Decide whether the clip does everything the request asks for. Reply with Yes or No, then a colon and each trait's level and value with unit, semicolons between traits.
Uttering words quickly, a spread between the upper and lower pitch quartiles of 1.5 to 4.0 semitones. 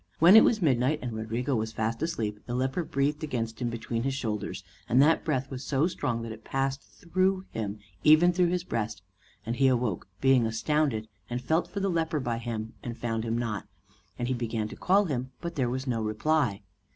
No: fast, 210 wpm; average, 5.2 semitones